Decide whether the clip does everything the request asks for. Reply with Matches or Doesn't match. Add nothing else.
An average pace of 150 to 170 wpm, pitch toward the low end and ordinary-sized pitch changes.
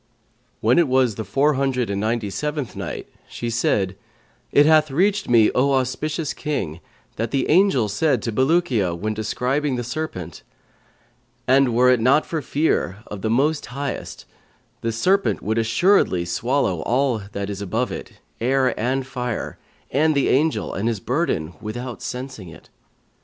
Matches